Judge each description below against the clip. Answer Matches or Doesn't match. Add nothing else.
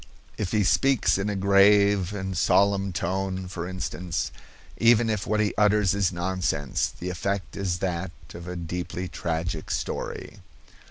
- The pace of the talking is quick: Doesn't match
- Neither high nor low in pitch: Doesn't match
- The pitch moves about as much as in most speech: Doesn't match